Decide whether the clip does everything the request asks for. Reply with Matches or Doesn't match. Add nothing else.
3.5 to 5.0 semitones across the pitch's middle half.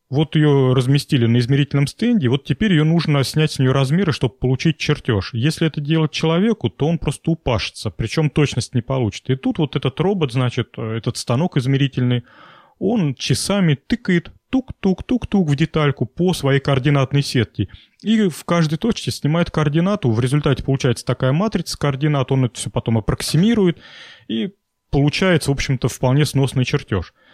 Matches